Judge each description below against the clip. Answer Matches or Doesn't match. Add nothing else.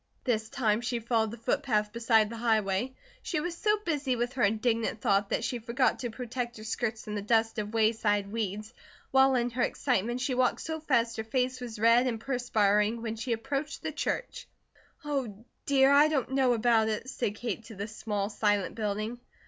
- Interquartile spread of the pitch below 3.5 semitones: Matches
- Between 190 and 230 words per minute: Matches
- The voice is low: Doesn't match